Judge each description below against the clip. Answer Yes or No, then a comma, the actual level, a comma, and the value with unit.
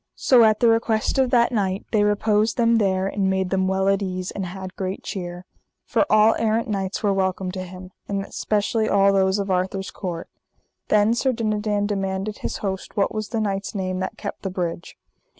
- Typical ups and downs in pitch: No, narrow, 2.2 semitones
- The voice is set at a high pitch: Yes, high, 195 Hz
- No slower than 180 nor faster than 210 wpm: Yes, average, 200 wpm